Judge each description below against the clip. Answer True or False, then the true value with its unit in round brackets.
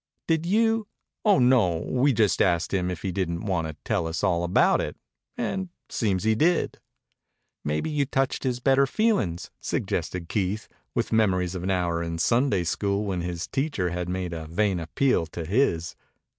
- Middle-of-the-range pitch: False (95 Hz)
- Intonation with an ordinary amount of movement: False (7.2 semitones)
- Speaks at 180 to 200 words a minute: True (185 wpm)